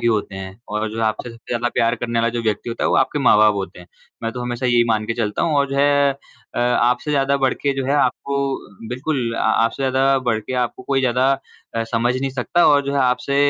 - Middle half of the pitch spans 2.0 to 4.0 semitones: Yes, average, 3.0 semitones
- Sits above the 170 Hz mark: No, low, 125 Hz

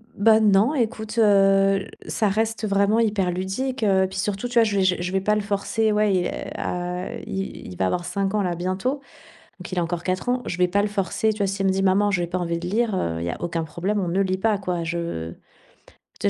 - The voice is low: No, high, 195 Hz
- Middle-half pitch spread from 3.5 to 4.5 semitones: No, average, 2.9 semitones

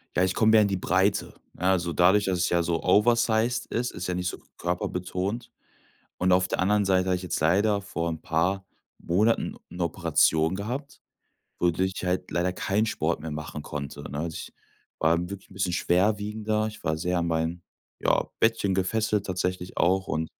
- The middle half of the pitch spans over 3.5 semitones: No, average, 3.0 semitones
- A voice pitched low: Yes, very low, 90 Hz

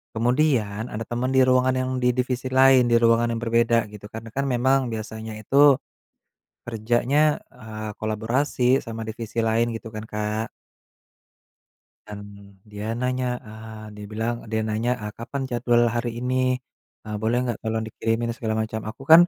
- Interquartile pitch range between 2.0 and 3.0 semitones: Yes, narrow, 2.5 semitones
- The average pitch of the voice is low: Yes, low, 115 Hz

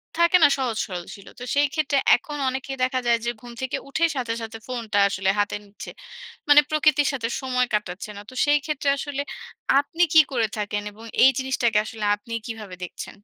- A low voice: No, very high, 250 Hz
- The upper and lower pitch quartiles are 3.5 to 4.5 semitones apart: No, average, 4.9 semitones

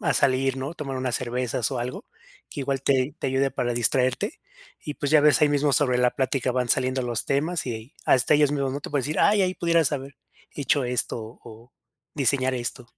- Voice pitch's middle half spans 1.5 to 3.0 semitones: Yes, narrow, 2.5 semitones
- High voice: No, low, 135 Hz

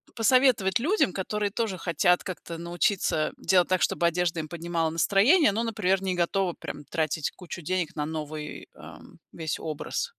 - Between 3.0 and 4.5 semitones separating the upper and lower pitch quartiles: Yes, average, 3.3 semitones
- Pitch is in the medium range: Yes, medium, 180 Hz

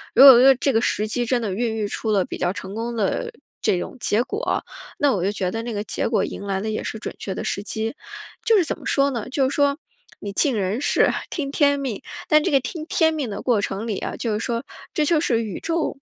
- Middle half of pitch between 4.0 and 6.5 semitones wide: Yes, average, 5.1 semitones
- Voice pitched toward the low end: No, high, 235 Hz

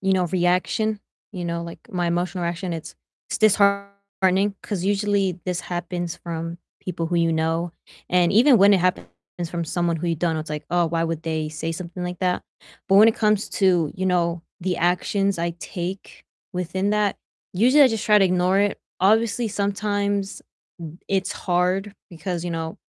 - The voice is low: No, medium, 180 Hz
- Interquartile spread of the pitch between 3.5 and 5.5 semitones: No, average, 2.8 semitones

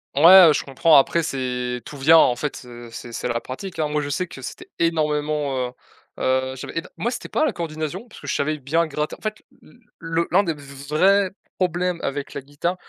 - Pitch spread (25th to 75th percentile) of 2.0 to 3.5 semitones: No, average, 4.0 semitones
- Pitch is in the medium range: Yes, medium, 150 Hz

